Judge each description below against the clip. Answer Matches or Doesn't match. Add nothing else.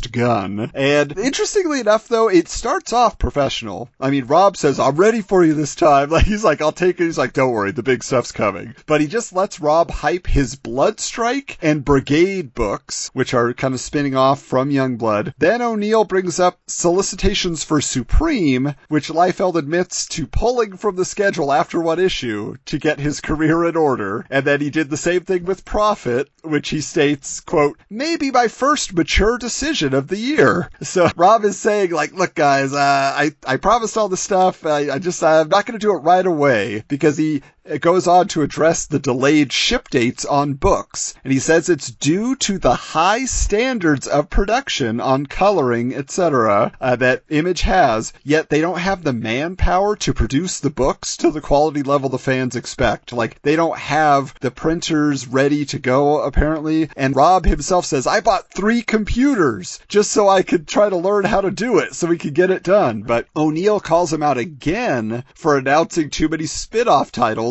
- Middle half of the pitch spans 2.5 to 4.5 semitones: Doesn't match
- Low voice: Doesn't match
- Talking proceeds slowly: Doesn't match